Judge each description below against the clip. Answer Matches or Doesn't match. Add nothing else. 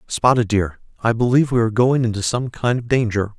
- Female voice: Doesn't match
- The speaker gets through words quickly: Matches